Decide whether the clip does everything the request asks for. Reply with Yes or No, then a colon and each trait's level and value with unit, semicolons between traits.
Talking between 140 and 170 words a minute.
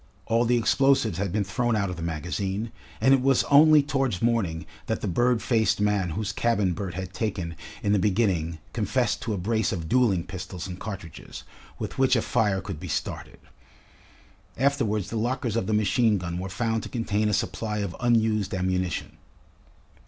No: average, 180 wpm